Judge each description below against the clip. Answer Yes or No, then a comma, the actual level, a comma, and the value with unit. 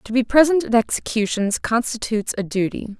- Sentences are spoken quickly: No, average, 160 wpm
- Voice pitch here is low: No, high, 230 Hz